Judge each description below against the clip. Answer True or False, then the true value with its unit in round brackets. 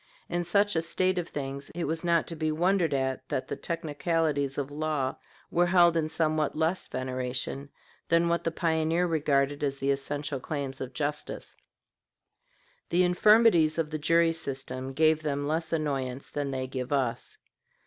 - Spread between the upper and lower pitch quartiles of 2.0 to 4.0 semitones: True (3.3 semitones)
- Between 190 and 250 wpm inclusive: False (165 wpm)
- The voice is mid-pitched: True (155 Hz)